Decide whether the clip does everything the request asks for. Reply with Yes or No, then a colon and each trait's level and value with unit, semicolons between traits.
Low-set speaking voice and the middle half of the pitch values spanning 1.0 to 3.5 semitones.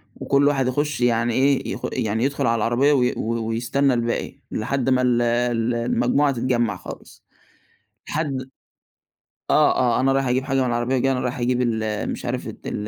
Yes: low, 125 Hz; narrow, 2.4 semitones